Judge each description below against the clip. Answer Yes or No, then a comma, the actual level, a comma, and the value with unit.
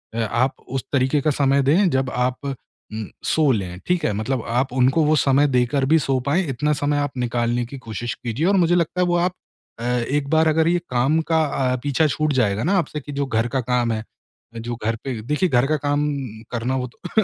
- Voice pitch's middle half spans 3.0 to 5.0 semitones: Yes, average, 4.1 semitones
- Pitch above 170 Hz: No, low, 135 Hz